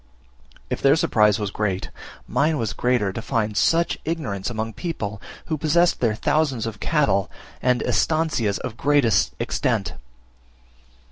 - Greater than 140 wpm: No, slow, 135 wpm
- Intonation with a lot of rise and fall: Yes, wide, 6.5 semitones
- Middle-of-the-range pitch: No, low, 120 Hz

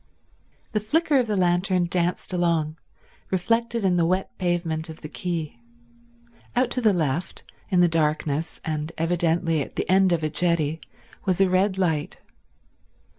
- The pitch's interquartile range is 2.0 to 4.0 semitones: Yes, average, 3.0 semitones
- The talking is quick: No, average, 155 wpm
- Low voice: No, medium, 175 Hz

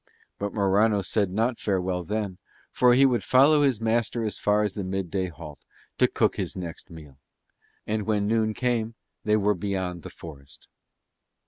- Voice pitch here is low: Yes, low, 105 Hz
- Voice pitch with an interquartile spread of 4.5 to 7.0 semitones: No, average, 3.4 semitones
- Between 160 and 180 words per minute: Yes, average, 165 wpm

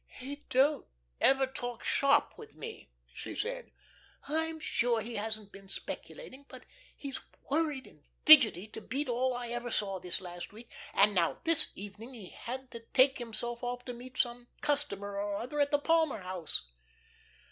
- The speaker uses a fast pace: No, average, 170 wpm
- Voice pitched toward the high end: Yes, high, 245 Hz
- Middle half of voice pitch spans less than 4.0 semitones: No, average, 5.0 semitones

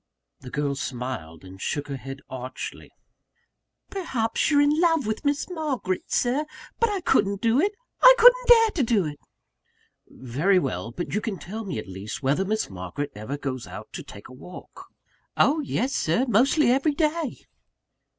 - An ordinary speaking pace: Yes, average, 170 wpm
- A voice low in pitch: No, high, 205 Hz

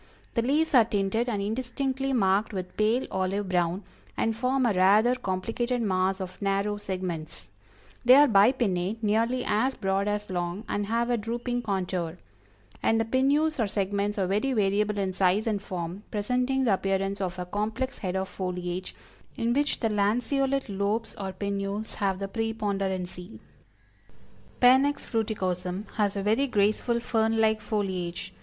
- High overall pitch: Yes, high, 205 Hz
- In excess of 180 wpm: No, average, 155 wpm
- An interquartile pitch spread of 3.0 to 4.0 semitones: Yes, average, 3.6 semitones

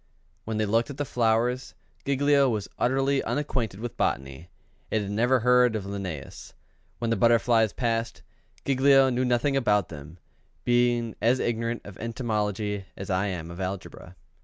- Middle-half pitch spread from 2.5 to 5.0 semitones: Yes, average, 3.5 semitones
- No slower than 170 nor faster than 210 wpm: No, average, 155 wpm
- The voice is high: No, low, 115 Hz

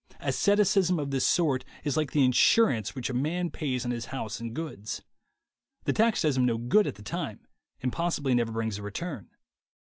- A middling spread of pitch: No, wide, 6.1 semitones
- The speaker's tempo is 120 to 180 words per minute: No, average, 190 wpm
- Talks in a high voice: No, low, 135 Hz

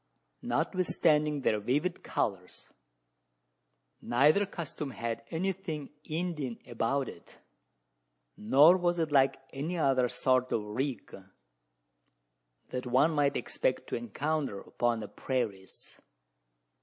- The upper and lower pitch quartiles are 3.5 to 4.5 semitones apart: No, average, 4.9 semitones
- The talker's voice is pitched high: No, medium, 140 Hz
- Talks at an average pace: No, slow, 105 wpm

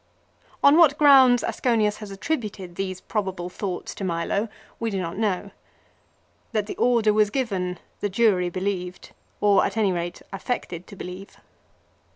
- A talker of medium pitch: No, high, 200 Hz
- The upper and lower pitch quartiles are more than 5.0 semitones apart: No, average, 3.6 semitones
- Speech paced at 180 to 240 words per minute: No, average, 150 wpm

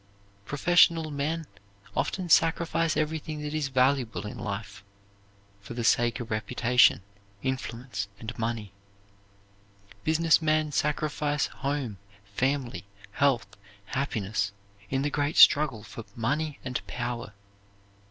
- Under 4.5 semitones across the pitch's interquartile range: No, average, 4.8 semitones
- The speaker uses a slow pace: Yes, slow, 110 wpm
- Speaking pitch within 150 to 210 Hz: No, low, 135 Hz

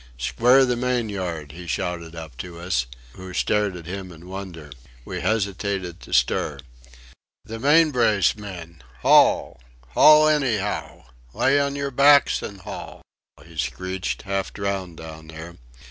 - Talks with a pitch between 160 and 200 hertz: No, very low, 95 Hz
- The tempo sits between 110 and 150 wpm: Yes, average, 145 wpm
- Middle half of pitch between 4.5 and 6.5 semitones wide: Yes, wide, 5.6 semitones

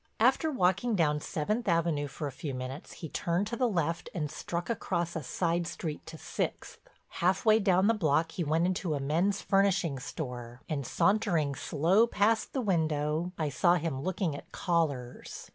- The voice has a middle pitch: Yes, medium, 170 Hz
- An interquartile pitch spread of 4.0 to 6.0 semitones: Yes, average, 4.4 semitones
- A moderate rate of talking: Yes, average, 180 wpm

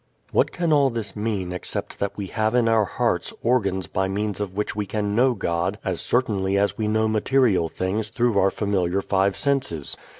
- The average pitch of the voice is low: Yes, low, 105 Hz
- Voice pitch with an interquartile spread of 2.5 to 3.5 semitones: Yes, average, 3.1 semitones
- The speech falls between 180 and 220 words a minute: Yes, average, 195 wpm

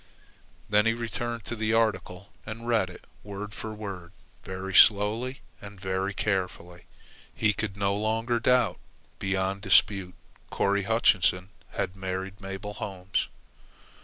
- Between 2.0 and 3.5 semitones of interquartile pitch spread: Yes, narrow, 2.6 semitones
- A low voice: Yes, low, 100 Hz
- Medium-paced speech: No, slow, 130 wpm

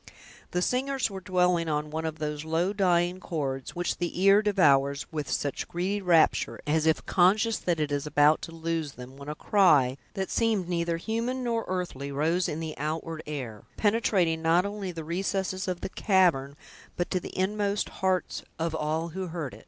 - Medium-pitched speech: Yes, medium, 170 Hz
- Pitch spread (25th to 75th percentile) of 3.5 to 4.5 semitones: Yes, average, 3.9 semitones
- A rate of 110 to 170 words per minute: No, average, 185 wpm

